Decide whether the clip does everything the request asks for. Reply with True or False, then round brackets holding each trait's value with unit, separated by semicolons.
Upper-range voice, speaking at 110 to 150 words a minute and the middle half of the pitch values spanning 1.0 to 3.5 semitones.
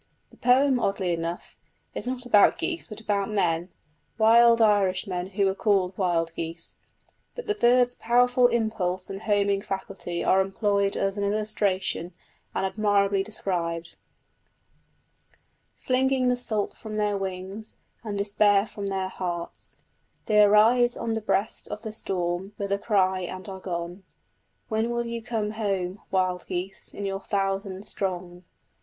True (200 Hz; 145 wpm; 2.8 semitones)